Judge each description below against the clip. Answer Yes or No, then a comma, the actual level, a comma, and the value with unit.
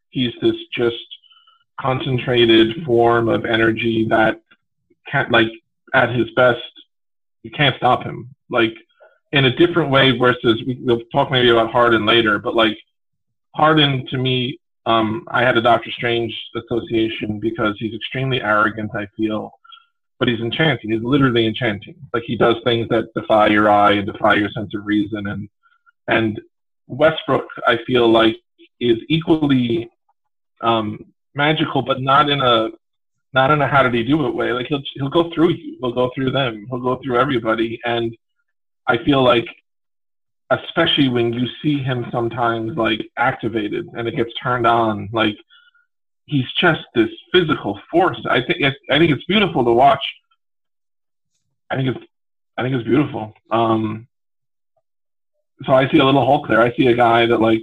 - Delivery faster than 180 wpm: No, average, 165 wpm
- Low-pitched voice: Yes, low, 120 Hz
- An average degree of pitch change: Yes, average, 4.1 semitones